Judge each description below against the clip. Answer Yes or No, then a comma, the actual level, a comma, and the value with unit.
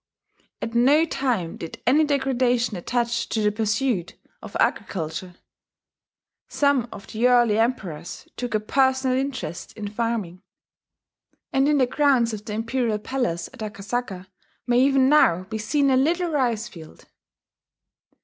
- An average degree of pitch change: Yes, average, 4.0 semitones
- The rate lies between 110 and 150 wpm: Yes, average, 140 wpm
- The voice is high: Yes, high, 235 Hz